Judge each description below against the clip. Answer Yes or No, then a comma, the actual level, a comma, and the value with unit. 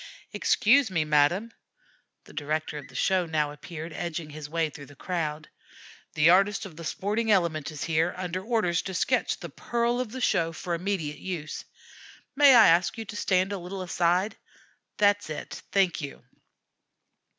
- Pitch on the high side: No, medium, 175 Hz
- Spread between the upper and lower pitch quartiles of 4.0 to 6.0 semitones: Yes, average, 4.4 semitones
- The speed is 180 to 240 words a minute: No, average, 170 wpm